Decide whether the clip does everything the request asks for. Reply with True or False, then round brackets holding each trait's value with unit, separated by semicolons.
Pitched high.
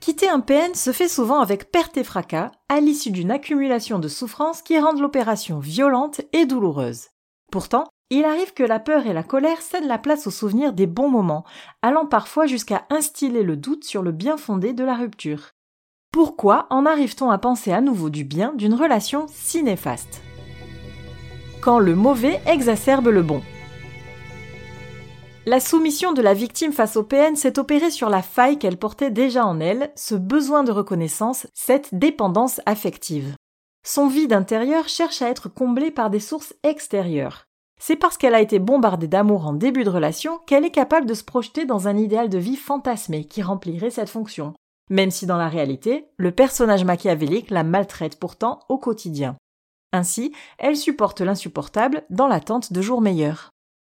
True (235 Hz)